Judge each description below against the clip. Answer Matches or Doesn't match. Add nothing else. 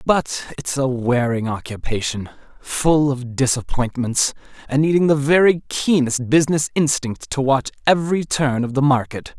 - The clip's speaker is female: Doesn't match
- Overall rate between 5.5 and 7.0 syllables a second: Doesn't match